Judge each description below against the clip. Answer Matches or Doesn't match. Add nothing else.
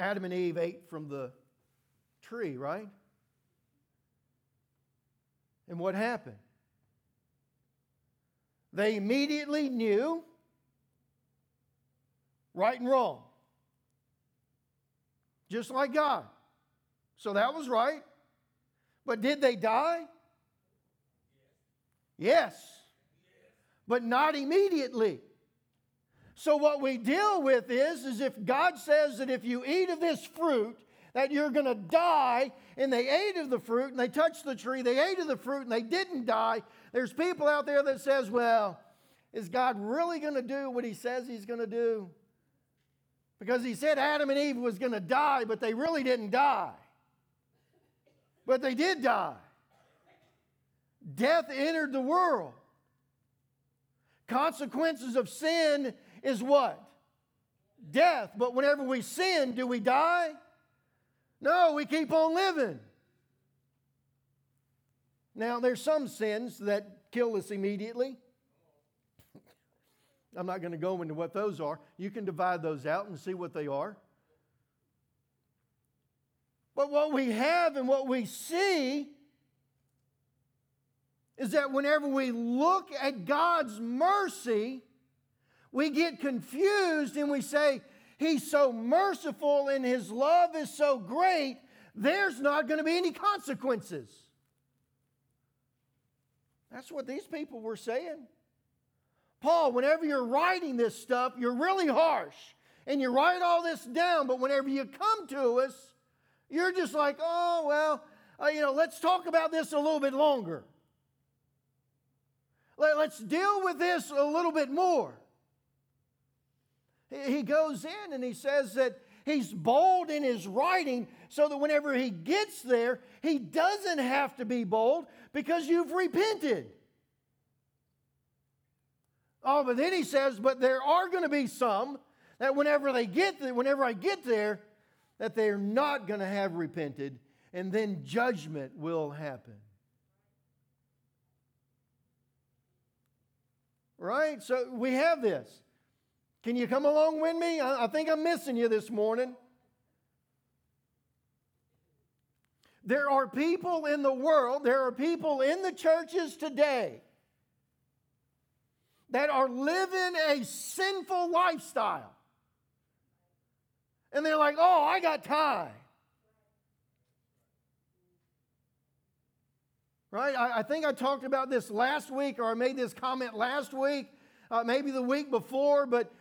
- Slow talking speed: Matches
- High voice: Matches